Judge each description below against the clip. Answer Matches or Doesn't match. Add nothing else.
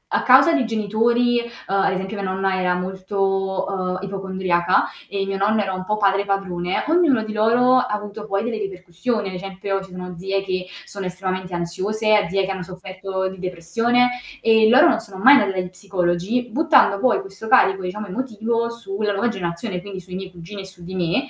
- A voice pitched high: Matches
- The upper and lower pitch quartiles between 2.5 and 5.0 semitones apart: Matches